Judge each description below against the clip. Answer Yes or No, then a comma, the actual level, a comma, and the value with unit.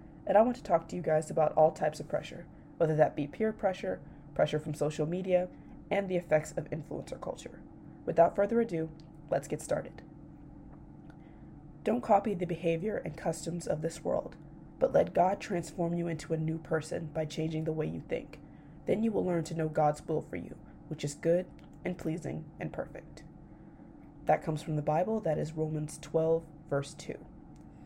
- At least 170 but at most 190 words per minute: Yes, average, 185 wpm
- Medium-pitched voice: Yes, medium, 160 Hz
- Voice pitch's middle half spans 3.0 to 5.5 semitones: No, narrow, 2.4 semitones